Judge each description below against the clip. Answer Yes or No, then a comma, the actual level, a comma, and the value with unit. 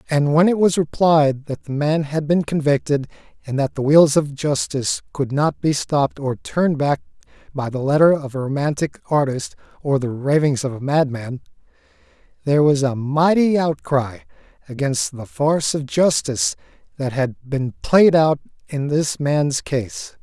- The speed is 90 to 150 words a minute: No, average, 165 wpm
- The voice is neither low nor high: Yes, medium, 145 Hz